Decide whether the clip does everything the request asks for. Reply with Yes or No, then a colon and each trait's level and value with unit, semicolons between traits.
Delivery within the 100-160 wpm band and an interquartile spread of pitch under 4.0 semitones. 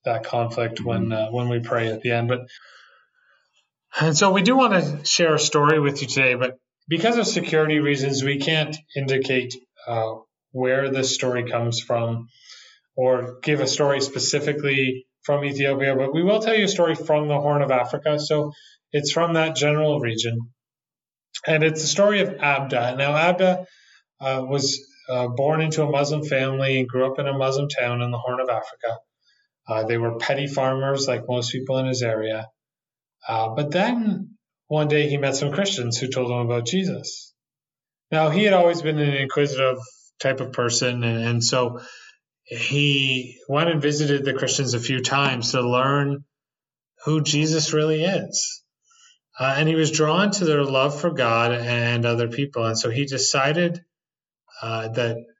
No: average, 175 wpm; average, 3.5 semitones